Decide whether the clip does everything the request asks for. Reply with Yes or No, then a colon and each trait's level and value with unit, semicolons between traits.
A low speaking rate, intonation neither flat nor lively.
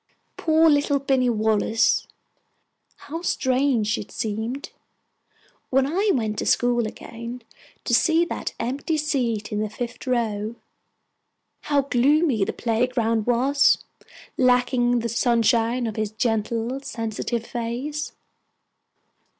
Yes: slow, 110 wpm; average, 3.4 semitones